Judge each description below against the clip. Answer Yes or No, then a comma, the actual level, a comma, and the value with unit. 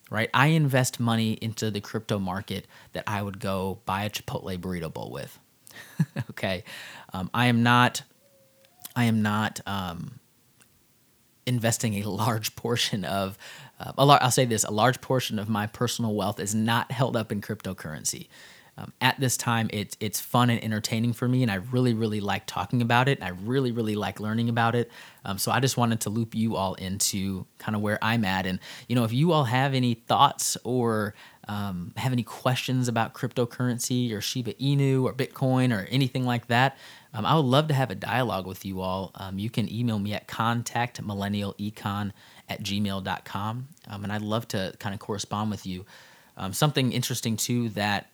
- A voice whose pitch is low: Yes, low, 115 Hz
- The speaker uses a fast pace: No, average, 190 wpm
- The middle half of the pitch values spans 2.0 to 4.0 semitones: Yes, average, 3.5 semitones